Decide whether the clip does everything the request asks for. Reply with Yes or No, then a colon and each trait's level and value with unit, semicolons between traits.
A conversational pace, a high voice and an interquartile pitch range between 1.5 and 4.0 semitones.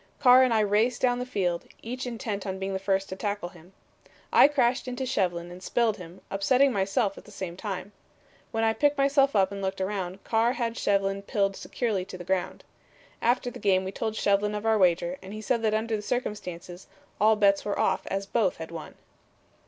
No: fast, 210 wpm; high, 205 Hz; average, 3.4 semitones